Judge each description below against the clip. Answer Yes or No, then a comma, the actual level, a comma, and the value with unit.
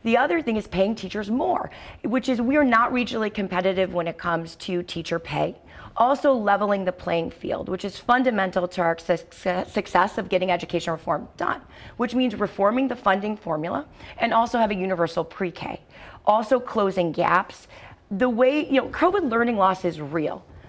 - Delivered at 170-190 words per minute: Yes, average, 175 wpm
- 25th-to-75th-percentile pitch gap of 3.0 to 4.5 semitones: No, wide, 5.5 semitones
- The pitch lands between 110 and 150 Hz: No, high, 200 Hz